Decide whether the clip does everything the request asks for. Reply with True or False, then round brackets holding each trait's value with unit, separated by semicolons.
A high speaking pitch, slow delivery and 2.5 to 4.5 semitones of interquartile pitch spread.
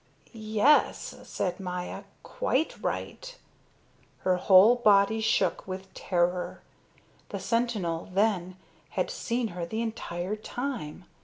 True (200 Hz; 105 wpm; 4.2 semitones)